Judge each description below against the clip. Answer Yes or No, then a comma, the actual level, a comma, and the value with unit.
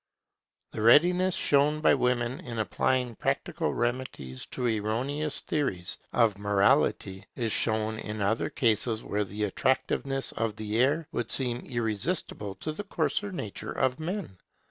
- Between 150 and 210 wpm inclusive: No, average, 140 wpm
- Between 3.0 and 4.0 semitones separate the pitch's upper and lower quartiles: No, average, 4.8 semitones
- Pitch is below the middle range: Yes, low, 120 Hz